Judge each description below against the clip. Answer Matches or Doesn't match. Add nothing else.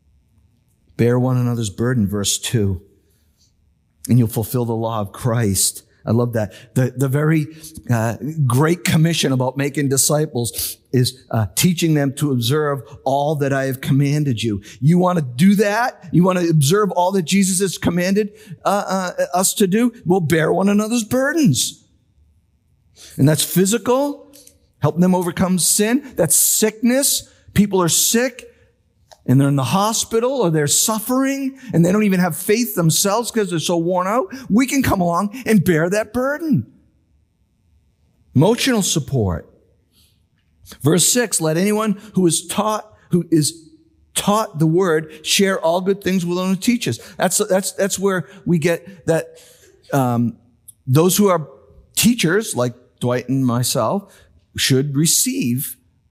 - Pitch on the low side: Doesn't match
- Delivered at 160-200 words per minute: Doesn't match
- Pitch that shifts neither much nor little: Doesn't match